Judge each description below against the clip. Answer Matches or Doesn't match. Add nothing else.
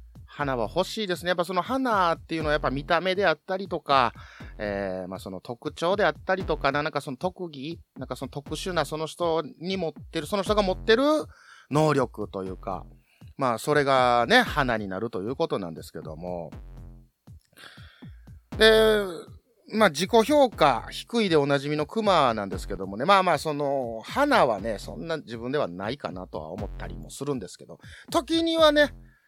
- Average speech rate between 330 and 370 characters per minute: Matches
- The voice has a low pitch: Doesn't match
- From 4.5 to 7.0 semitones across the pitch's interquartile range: Doesn't match